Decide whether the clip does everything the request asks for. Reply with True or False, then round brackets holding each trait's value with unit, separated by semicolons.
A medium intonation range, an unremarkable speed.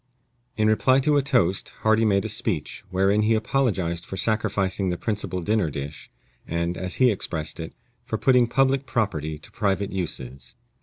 True (4.6 semitones; 165 wpm)